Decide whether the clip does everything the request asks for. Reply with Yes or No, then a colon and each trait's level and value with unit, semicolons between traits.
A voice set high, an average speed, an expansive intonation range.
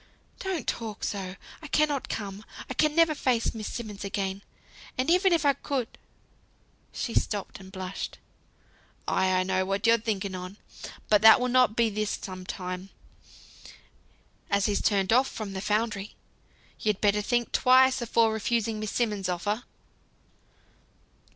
No: high, 215 Hz; average, 150 wpm; average, 3.8 semitones